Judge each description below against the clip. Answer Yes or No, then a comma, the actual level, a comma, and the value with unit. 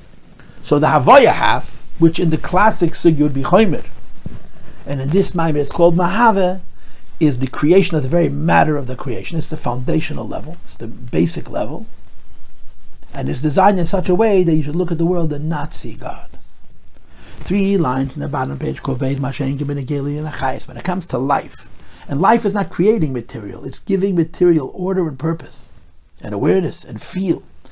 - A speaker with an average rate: Yes, average, 175 wpm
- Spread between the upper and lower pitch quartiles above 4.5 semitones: Yes, average, 4.9 semitones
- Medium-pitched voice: Yes, medium, 155 Hz